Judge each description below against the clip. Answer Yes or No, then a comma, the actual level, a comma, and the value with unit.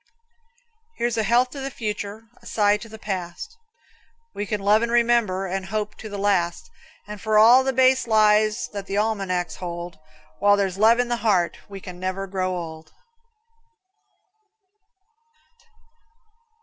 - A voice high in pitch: Yes, high, 210 Hz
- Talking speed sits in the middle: Yes, average, 150 wpm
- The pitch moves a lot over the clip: No, average, 3.1 semitones